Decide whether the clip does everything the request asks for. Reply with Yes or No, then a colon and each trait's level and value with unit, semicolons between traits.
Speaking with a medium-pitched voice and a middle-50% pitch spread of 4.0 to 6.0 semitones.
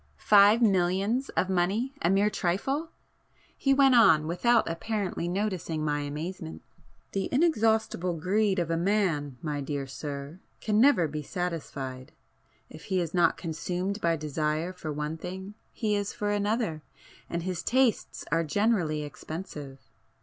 Yes: medium, 180 Hz; average, 5.2 semitones